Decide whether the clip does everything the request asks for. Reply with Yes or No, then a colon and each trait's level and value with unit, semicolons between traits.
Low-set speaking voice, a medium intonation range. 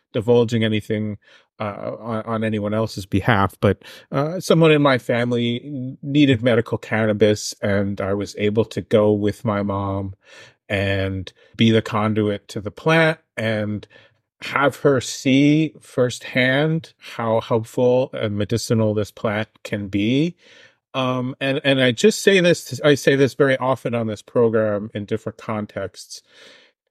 Yes: low, 115 Hz; average, 3.8 semitones